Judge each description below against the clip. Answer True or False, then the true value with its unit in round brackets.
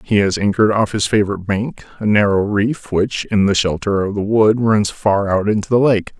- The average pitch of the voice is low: True (105 Hz)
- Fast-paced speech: True (225 wpm)